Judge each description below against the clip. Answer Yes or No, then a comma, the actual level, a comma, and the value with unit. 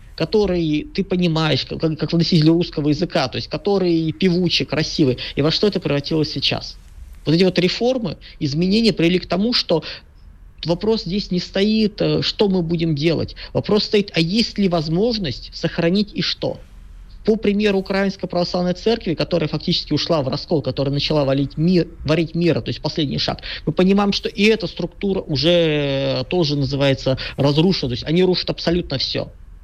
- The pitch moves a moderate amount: Yes, average, 4.0 semitones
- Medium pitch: Yes, medium, 165 Hz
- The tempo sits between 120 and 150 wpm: No, fast, 160 wpm